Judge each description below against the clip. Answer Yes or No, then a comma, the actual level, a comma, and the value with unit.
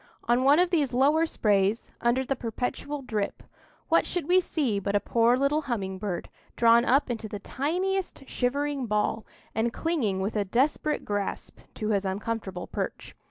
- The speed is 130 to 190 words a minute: Yes, average, 165 wpm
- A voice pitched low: No, high, 240 Hz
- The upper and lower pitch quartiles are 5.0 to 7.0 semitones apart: Yes, wide, 5.6 semitones